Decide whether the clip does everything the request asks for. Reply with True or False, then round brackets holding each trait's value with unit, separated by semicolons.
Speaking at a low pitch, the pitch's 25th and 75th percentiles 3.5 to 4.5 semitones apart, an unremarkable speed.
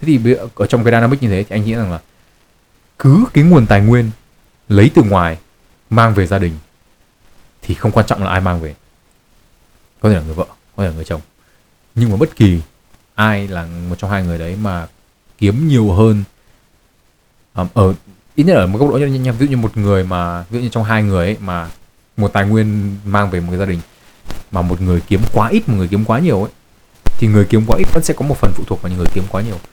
True (100 Hz; 4.2 semitones; 240 wpm)